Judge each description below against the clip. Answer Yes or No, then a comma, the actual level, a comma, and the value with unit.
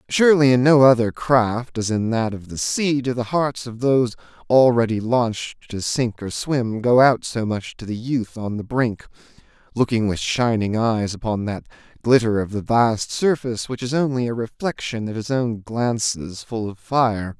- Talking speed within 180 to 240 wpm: Yes, average, 190 wpm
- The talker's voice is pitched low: Yes, low, 120 Hz